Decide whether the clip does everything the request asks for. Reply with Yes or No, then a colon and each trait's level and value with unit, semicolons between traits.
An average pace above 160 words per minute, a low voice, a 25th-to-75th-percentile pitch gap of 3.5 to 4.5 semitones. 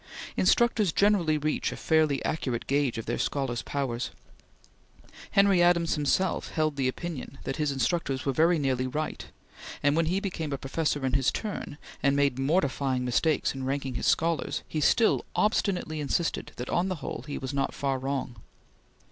No: average, 170 wpm; medium, 145 Hz; average, 3.9 semitones